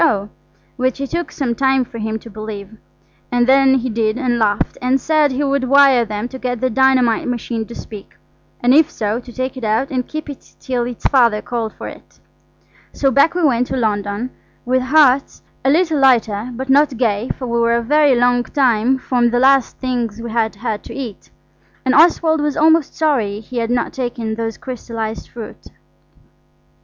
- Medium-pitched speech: No, high, 245 Hz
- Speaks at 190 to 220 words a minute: Yes, average, 195 wpm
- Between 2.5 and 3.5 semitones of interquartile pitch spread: Yes, average, 2.8 semitones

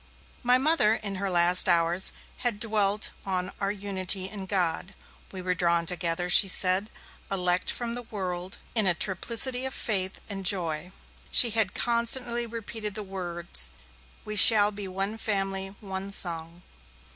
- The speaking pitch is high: Yes, high, 195 Hz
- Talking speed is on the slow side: No, average, 150 wpm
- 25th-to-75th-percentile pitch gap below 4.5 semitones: Yes, average, 3.0 semitones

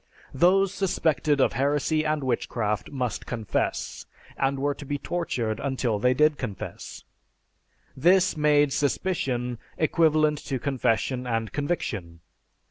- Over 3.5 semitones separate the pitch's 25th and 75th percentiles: Yes, average, 3.9 semitones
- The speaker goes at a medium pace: No, slow, 120 wpm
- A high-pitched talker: No, medium, 140 Hz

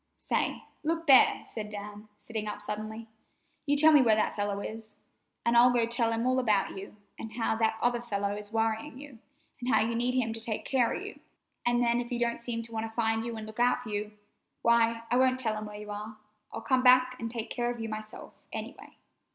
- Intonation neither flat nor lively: No, narrow, 2.0 semitones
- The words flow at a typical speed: No, fast, 235 wpm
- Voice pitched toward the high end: Yes, high, 230 Hz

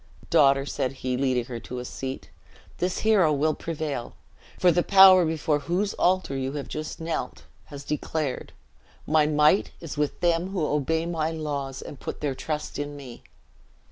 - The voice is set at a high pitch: No, medium, 150 Hz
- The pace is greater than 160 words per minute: Yes, average, 170 wpm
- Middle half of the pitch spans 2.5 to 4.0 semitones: Yes, average, 3.2 semitones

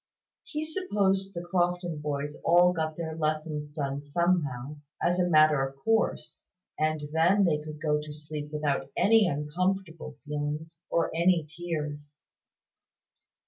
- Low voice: No, medium, 155 Hz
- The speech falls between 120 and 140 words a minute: Yes, slow, 135 wpm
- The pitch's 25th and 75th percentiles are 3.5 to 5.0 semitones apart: No, average, 3.0 semitones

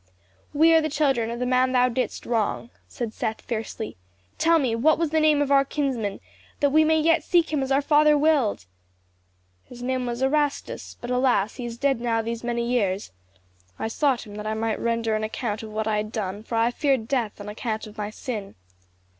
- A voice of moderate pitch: No, high, 245 Hz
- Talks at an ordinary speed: No, fast, 215 wpm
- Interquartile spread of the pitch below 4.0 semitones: No, average, 4.4 semitones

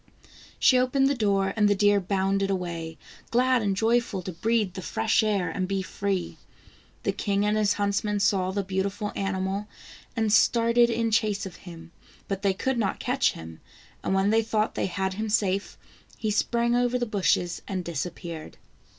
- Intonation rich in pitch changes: No, average, 2.7 semitones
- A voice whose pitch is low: No, high, 200 Hz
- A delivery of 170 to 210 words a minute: Yes, average, 175 wpm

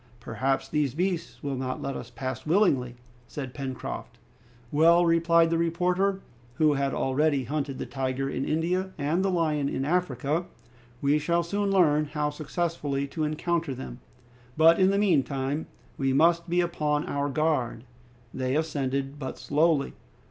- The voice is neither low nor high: Yes, medium, 150 Hz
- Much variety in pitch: No, average, 3.7 semitones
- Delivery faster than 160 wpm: No, average, 155 wpm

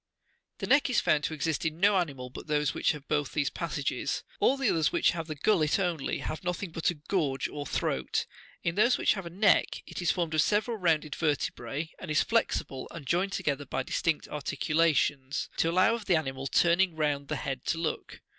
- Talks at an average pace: No, fast, 210 wpm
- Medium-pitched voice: Yes, medium, 160 Hz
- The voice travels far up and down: No, average, 3.6 semitones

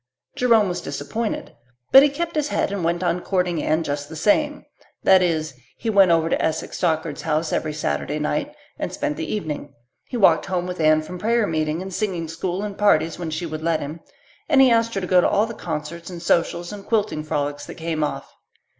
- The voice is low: No, medium, 170 Hz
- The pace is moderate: No, fast, 215 wpm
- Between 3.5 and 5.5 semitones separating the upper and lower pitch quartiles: Yes, average, 4.5 semitones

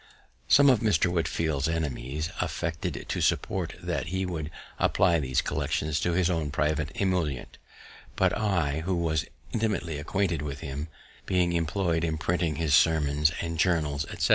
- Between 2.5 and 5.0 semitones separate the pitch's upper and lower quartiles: Yes, average, 2.8 semitones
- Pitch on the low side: Yes, very low, 80 Hz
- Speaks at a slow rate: No, average, 155 wpm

